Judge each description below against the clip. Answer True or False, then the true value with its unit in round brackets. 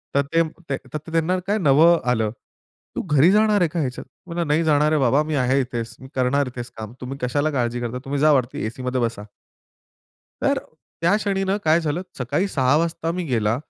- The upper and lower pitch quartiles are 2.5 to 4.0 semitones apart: False (4.8 semitones)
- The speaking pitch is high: False (145 Hz)